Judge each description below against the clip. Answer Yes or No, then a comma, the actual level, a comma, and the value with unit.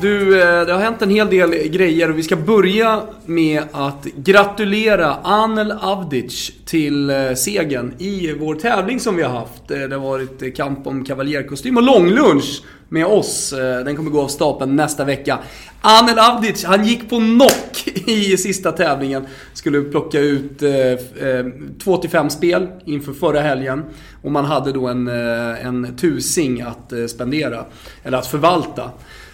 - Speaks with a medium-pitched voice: Yes, medium, 155 Hz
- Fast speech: No, average, 145 wpm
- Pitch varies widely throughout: Yes, wide, 6.1 semitones